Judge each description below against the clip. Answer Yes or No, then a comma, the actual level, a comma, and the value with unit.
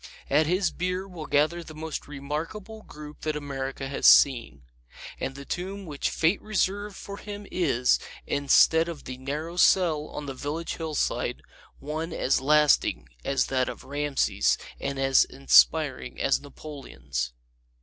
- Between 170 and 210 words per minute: No, average, 145 wpm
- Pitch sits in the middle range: Yes, medium, 150 Hz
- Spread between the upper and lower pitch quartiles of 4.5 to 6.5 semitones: No, average, 3.7 semitones